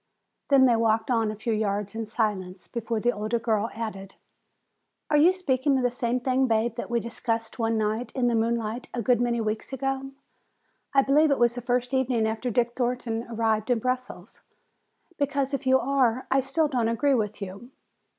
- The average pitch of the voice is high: Yes, high, 235 Hz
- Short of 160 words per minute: No, average, 190 wpm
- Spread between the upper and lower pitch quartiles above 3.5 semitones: No, average, 2.8 semitones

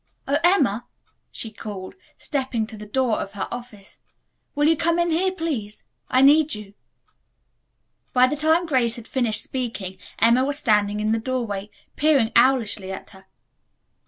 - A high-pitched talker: Yes, high, 240 Hz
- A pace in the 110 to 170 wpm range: Yes, average, 160 wpm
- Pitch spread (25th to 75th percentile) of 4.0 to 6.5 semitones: Yes, wide, 5.5 semitones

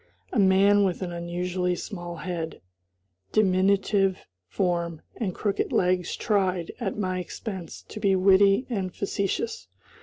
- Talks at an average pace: No, slow, 125 wpm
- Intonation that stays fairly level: Yes, narrow, 2.1 semitones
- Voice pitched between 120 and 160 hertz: No, high, 190 Hz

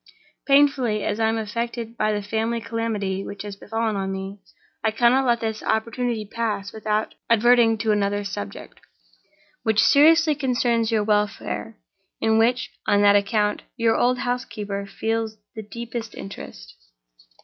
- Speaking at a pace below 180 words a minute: Yes, average, 150 wpm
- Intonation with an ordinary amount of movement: No, narrow, 2.2 semitones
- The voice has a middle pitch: No, high, 220 Hz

